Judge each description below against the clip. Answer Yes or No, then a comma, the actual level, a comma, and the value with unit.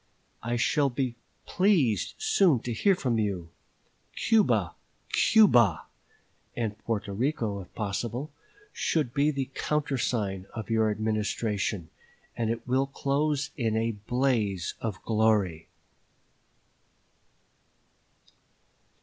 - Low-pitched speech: Yes, low, 115 Hz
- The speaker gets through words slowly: Yes, slow, 100 wpm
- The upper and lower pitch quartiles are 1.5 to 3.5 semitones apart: No, average, 4.7 semitones